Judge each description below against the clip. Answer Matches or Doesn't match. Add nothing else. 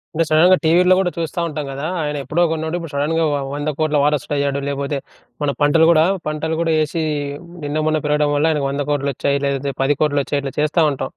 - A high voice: Doesn't match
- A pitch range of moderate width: Doesn't match